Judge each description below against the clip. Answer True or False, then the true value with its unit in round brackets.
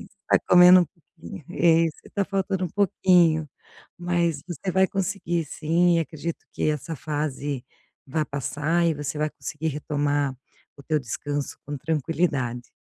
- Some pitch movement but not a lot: True (3.2 semitones)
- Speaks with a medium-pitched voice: True (160 Hz)